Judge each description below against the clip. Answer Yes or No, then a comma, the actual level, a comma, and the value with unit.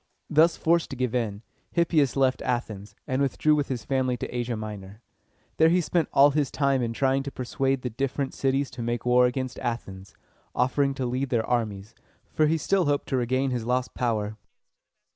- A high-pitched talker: No, low, 130 Hz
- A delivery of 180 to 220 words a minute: Yes, average, 190 wpm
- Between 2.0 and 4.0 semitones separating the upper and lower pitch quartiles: Yes, average, 2.7 semitones